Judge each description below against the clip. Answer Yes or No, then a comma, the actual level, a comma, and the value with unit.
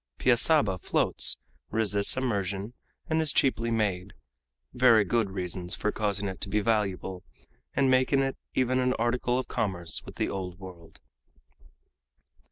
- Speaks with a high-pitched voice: No, low, 105 Hz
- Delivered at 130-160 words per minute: Yes, average, 140 wpm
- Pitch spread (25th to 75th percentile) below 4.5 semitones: No, average, 4.9 semitones